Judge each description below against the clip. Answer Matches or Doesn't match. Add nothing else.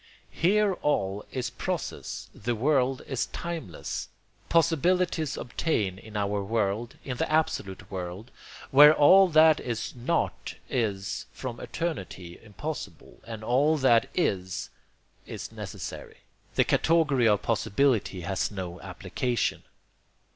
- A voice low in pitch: Matches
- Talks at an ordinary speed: Doesn't match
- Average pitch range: Doesn't match